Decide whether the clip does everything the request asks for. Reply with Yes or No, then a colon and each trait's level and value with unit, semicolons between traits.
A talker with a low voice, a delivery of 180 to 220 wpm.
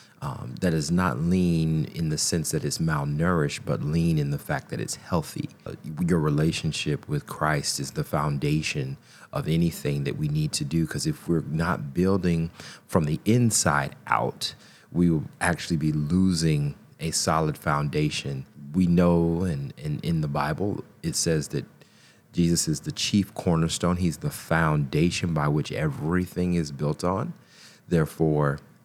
No: very low, 85 Hz; average, 160 wpm